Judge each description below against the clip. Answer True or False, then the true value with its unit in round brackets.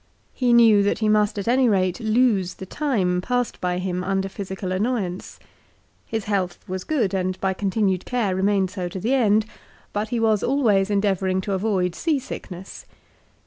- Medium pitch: False (200 Hz)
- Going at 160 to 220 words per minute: True (175 wpm)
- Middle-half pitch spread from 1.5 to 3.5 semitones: True (3.2 semitones)